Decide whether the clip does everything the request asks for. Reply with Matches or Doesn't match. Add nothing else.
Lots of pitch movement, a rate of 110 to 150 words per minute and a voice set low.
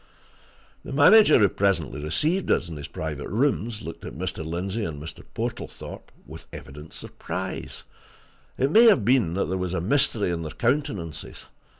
Doesn't match